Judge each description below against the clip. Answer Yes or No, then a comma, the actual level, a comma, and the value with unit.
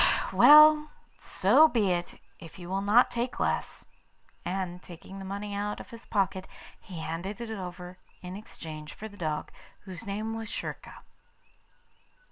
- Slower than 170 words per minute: Yes, average, 150 wpm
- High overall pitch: Yes, high, 195 Hz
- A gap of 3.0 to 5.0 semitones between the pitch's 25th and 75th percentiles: Yes, average, 3.7 semitones